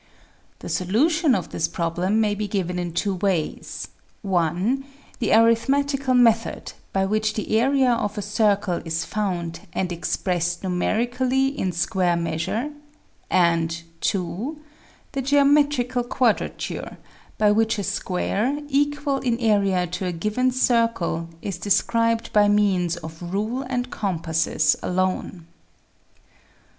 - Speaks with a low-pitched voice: No, high, 205 Hz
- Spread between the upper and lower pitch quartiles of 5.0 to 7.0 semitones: Yes, wide, 5.6 semitones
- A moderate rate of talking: No, slow, 125 wpm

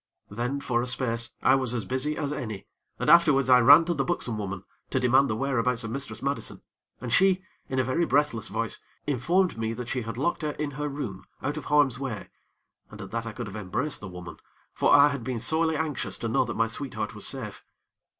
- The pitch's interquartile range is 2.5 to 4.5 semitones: Yes, average, 4.2 semitones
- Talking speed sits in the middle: No, fast, 225 wpm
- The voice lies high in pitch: No, low, 130 Hz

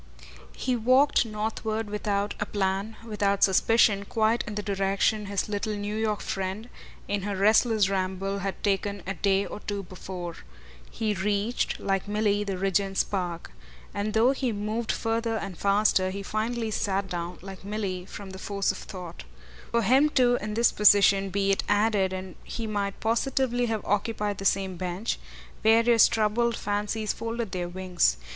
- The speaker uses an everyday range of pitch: No, narrow, 2.2 semitones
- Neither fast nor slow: Yes, average, 165 wpm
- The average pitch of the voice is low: No, high, 205 Hz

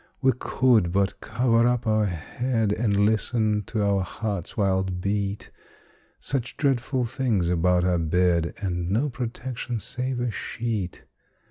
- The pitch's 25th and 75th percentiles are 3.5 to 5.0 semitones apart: Yes, average, 4.5 semitones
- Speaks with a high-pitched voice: No, low, 105 Hz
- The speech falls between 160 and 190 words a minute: No, slow, 135 wpm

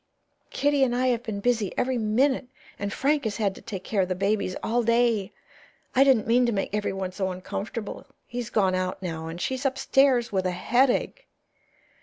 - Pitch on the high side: Yes, high, 220 Hz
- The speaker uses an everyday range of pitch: Yes, average, 4.5 semitones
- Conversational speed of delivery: Yes, average, 190 wpm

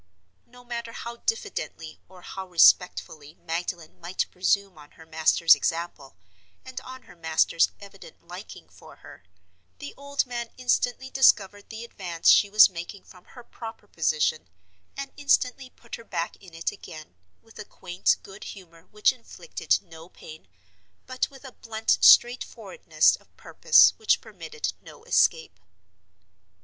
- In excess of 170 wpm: No, average, 145 wpm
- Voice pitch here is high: Yes, high, 200 Hz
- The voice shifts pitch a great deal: Yes, wide, 6.8 semitones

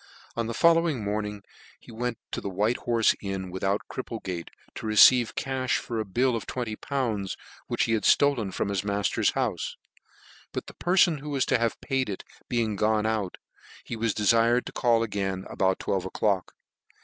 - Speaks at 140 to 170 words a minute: No, average, 185 wpm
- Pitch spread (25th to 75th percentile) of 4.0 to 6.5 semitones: No, average, 3.5 semitones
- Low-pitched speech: Yes, low, 110 Hz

